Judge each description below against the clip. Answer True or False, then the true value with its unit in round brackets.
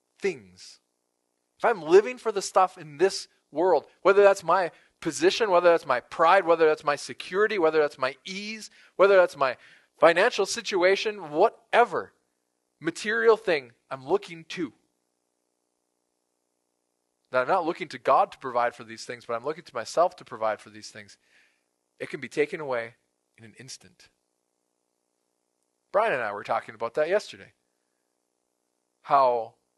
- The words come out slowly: False (150 wpm)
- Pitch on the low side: True (120 Hz)